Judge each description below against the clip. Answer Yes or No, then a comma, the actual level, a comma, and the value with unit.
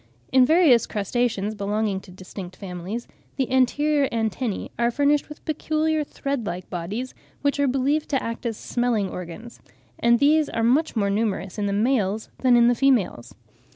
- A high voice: Yes, high, 235 Hz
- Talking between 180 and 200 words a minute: No, average, 165 wpm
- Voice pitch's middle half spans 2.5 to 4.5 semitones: No, average, 5.3 semitones